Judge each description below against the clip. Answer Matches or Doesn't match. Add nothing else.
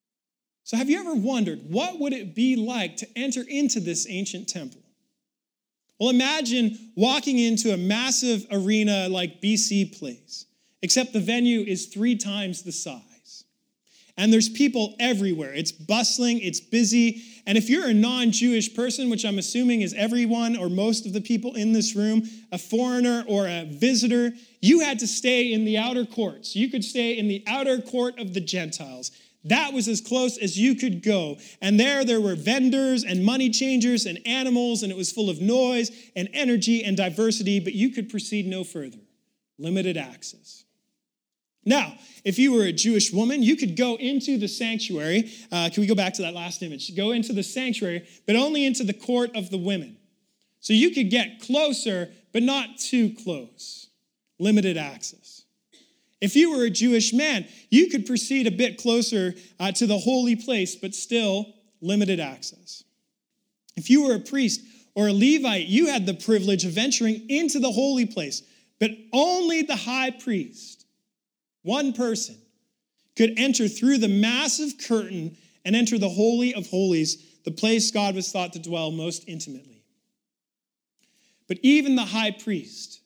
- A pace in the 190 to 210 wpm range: Doesn't match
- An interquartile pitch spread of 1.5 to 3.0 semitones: Doesn't match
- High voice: Matches